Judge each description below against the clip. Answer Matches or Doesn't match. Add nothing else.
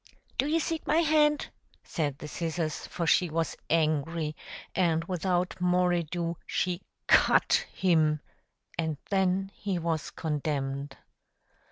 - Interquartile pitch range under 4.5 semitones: Matches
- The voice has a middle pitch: Matches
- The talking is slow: Matches